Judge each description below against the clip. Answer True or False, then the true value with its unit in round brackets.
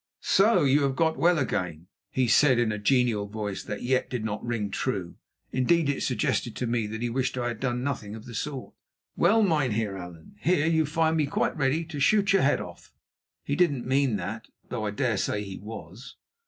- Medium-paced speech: False (210 wpm)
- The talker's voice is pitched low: True (125 Hz)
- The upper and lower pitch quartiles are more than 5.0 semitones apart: True (5.4 semitones)